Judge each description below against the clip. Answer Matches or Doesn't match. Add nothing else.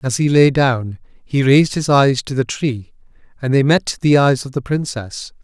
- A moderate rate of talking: Doesn't match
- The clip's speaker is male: Matches